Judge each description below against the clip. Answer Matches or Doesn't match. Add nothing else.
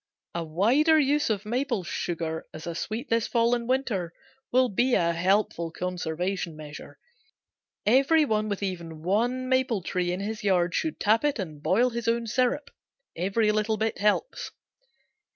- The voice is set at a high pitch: Matches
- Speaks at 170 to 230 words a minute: Doesn't match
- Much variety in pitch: Matches